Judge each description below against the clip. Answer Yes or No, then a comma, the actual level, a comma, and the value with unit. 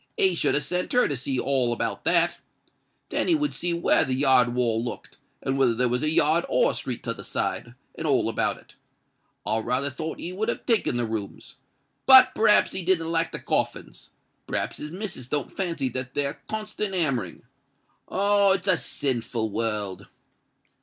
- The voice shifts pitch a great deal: Yes, wide, 7.0 semitones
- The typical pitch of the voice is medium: Yes, medium, 145 Hz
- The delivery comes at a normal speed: Yes, average, 180 wpm